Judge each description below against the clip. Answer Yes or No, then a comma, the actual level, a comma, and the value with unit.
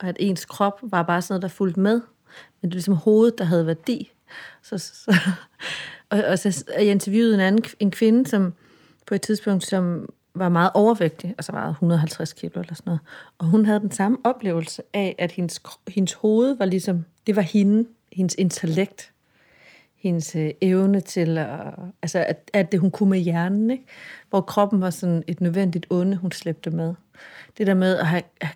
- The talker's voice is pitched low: No, high, 190 Hz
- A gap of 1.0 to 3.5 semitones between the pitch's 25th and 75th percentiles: Yes, average, 3.0 semitones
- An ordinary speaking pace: Yes, average, 195 wpm